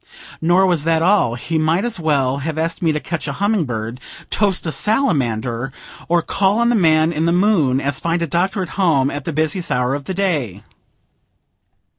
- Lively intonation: No, average, 5.0 semitones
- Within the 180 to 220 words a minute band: Yes, average, 200 wpm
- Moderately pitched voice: Yes, medium, 160 Hz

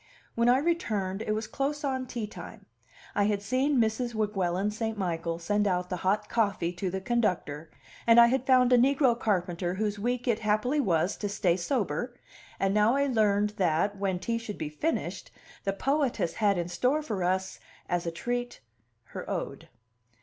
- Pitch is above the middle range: Yes, high, 210 Hz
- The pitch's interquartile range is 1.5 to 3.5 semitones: No, average, 4.6 semitones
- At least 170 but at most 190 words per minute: Yes, average, 180 wpm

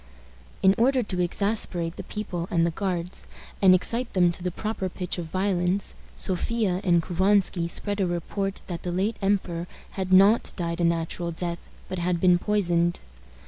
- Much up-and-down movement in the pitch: No, narrow, 2.5 semitones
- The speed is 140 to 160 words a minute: No, average, 170 wpm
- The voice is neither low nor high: Yes, medium, 180 Hz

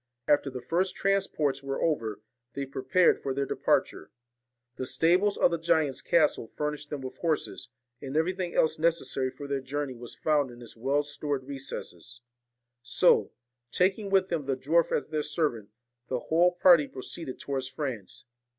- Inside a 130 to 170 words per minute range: Yes, average, 160 wpm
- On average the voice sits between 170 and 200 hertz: No, medium, 145 Hz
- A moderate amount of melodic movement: Yes, average, 4.1 semitones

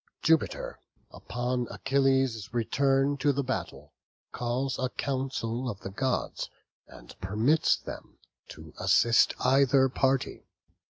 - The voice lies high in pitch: No, low, 130 Hz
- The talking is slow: Yes, slow, 110 wpm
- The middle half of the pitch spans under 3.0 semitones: Yes, narrow, 2.5 semitones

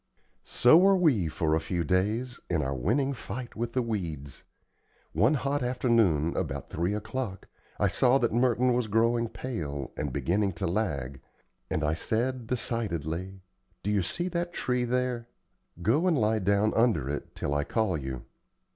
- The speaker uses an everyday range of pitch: No, wide, 6.8 semitones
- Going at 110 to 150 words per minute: No, average, 165 wpm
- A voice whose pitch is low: Yes, low, 110 Hz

